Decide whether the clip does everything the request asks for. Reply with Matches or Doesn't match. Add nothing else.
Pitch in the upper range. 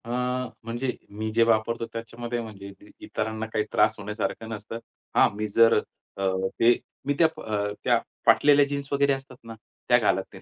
Doesn't match